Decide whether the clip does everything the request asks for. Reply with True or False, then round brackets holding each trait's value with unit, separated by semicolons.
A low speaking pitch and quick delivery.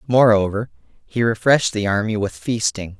False (110 Hz; 140 wpm)